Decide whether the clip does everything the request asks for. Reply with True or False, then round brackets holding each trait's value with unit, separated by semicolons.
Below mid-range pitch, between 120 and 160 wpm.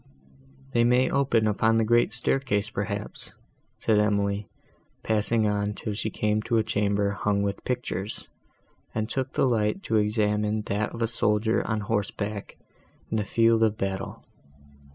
True (105 Hz; 155 wpm)